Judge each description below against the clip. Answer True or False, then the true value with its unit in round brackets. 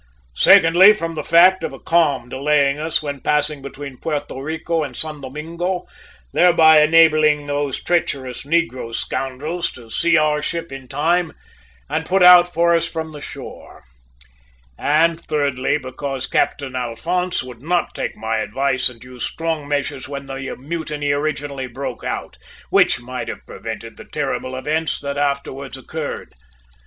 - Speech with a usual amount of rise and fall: True (3.4 semitones)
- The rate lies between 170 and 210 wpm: False (150 wpm)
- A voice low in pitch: False (145 Hz)